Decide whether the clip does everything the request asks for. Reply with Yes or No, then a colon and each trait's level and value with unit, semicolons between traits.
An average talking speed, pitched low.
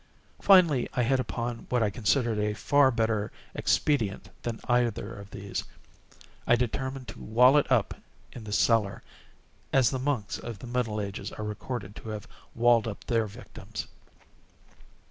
Yes: average, 150 wpm; low, 115 Hz